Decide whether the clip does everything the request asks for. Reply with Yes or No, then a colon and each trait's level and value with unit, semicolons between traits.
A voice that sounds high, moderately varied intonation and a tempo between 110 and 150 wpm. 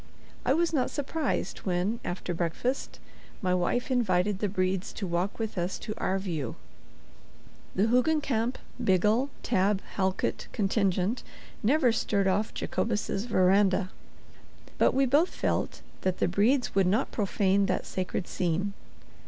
Yes: high, 200 Hz; average, 4.3 semitones; slow, 135 wpm